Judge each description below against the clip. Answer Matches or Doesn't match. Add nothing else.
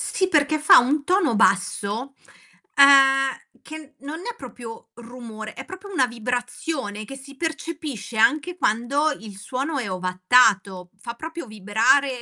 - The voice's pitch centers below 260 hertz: Doesn't match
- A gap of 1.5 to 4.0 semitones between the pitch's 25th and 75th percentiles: Doesn't match